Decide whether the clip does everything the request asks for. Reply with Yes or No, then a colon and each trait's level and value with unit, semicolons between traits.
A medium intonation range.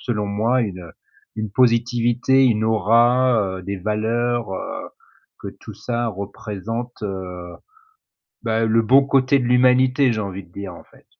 Yes: average, 3.5 semitones